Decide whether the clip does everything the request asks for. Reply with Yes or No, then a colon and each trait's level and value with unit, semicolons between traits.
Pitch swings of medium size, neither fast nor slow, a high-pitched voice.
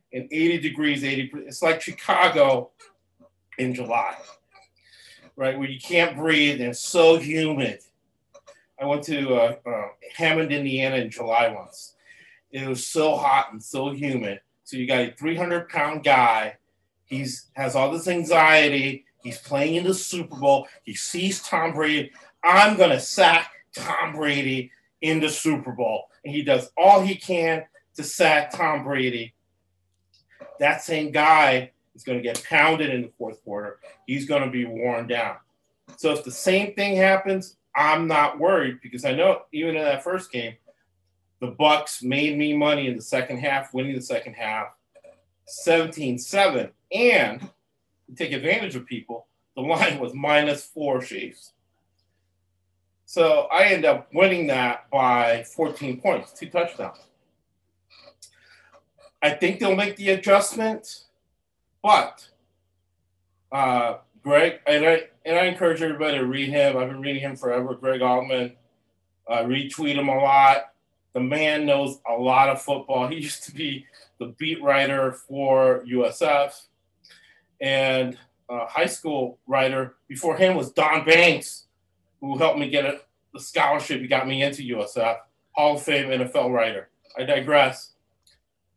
No: average, 4.5 semitones; average, 155 wpm; low, 135 Hz